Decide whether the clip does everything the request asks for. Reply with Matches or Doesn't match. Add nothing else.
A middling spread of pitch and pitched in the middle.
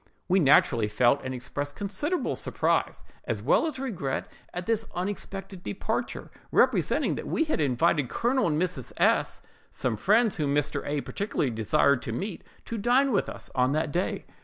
Doesn't match